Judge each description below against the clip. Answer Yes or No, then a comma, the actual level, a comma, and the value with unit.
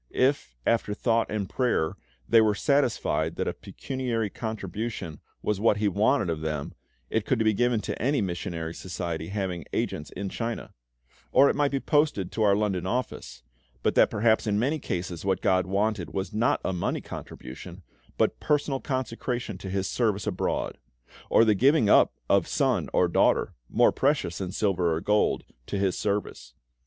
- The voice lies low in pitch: Yes, low, 105 Hz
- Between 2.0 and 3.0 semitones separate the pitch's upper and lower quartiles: No, average, 4.4 semitones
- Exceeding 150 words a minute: Yes, average, 170 wpm